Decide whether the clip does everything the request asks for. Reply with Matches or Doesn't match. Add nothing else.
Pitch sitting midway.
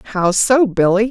Doesn't match